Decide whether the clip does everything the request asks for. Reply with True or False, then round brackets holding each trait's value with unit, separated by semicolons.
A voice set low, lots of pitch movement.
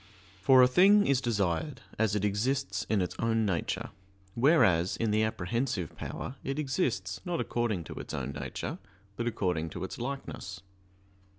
True (110 Hz; 5.7 semitones)